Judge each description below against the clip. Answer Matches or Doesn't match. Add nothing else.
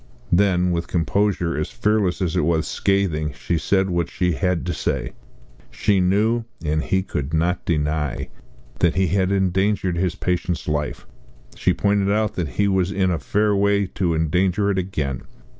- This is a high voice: Doesn't match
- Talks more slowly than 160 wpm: Doesn't match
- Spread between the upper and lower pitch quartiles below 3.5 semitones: Matches